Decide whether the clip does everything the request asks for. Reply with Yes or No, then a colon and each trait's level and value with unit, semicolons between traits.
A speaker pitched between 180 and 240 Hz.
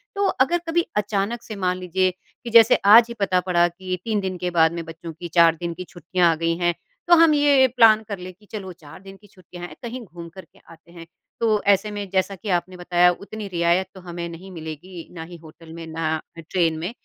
Yes: medium, 185 Hz